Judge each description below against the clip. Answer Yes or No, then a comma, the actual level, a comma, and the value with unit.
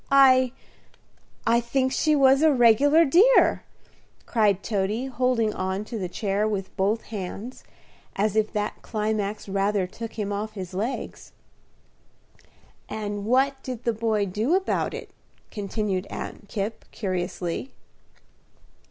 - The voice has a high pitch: Yes, high, 215 Hz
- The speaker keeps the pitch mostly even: No, average, 4.1 semitones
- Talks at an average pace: No, slow, 125 wpm